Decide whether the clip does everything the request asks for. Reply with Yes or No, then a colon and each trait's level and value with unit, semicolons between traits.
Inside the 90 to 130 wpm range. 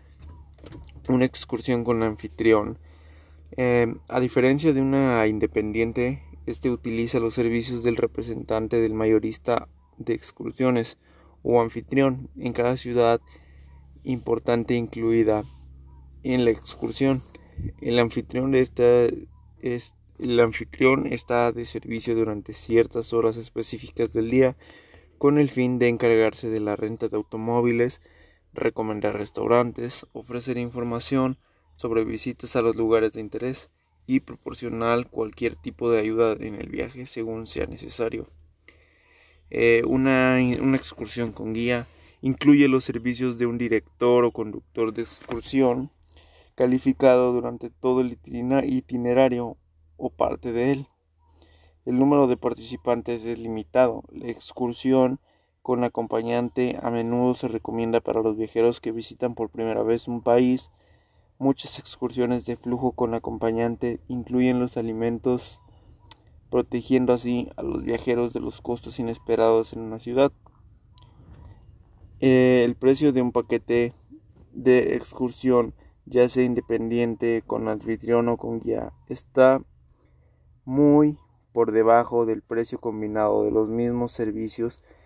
Yes: slow, 125 wpm